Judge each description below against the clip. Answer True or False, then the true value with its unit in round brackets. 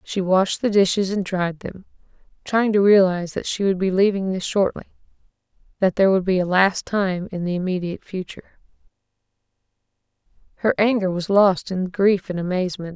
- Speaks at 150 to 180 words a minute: True (160 wpm)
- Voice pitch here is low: False (190 Hz)